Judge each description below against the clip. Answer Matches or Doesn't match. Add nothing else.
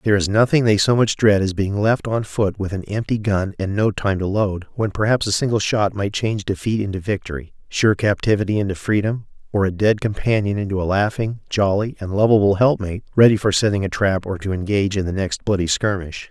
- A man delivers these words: Matches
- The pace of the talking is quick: Matches